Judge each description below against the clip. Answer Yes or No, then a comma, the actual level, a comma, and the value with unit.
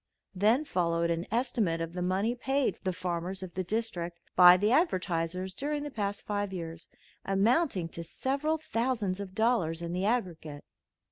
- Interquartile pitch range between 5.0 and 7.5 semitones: Yes, average, 5.3 semitones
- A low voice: No, high, 190 Hz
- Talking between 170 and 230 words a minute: No, average, 160 wpm